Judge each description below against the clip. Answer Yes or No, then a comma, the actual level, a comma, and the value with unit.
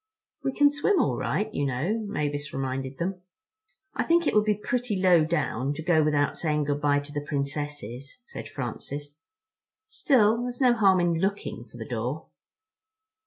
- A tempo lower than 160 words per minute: No, average, 170 wpm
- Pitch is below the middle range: No, medium, 155 Hz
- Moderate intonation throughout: No, wide, 6.9 semitones